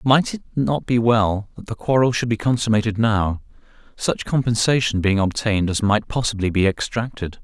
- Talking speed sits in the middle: Yes, average, 160 wpm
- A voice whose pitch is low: Yes, low, 110 Hz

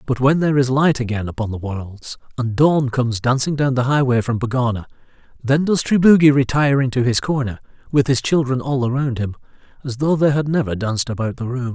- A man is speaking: Yes, male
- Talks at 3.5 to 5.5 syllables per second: No, 5.8 syllables/s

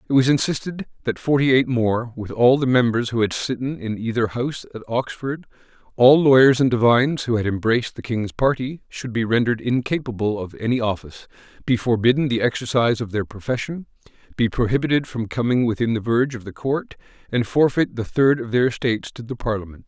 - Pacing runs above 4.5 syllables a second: Yes, 5.9 syllables/s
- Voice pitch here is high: No, low, 120 Hz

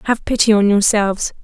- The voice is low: No, high, 215 Hz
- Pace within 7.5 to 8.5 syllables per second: No, 5.8 syllables/s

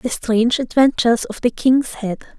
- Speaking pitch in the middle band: No, high, 245 Hz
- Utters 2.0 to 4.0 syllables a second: No, 5.1 syllables/s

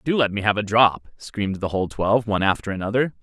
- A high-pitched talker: No, low, 105 Hz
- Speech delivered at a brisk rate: Yes, fast, 240 wpm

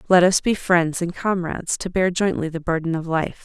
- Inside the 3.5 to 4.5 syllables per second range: No, 5.2 syllables/s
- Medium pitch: Yes, medium, 175 Hz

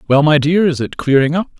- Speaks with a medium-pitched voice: Yes, medium, 150 Hz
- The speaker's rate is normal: No, fast, 265 wpm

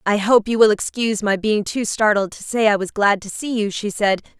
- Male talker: No, female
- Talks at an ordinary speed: No, fast, 260 wpm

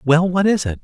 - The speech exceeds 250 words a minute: Yes, fast, 285 wpm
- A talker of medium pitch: Yes, medium, 165 Hz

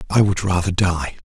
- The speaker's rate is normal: Yes, average, 190 wpm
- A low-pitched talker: Yes, very low, 90 Hz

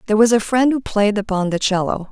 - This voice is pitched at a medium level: No, high, 210 Hz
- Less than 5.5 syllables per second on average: No, 6.3 syllables/s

